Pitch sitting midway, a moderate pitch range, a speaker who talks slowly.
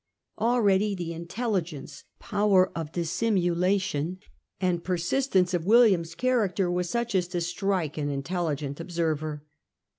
Yes: medium, 180 Hz; average, 3.2 semitones; slow, 120 wpm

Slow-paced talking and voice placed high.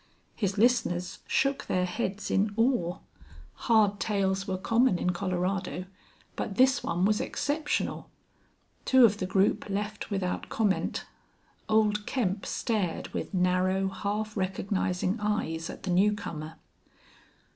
Yes: slow, 125 wpm; high, 200 Hz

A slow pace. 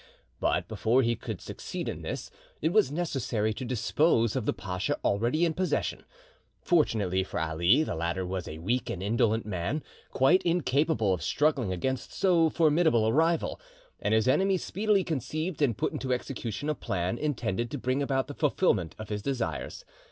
No: average, 175 wpm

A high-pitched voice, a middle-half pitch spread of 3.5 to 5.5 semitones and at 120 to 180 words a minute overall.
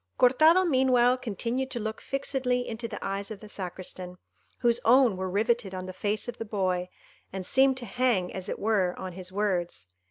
No: high, 215 Hz; average, 5.0 semitones; average, 190 wpm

